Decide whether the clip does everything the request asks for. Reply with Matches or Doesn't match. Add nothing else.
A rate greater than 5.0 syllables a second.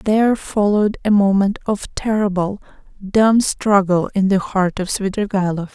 Doesn't match